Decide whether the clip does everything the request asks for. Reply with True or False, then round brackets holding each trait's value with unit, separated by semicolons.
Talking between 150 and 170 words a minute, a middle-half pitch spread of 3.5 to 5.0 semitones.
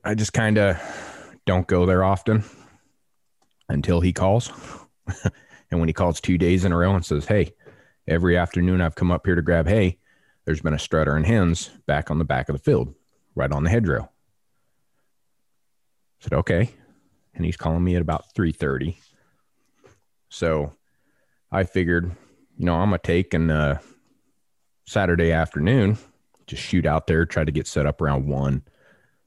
False (165 wpm; 3.0 semitones)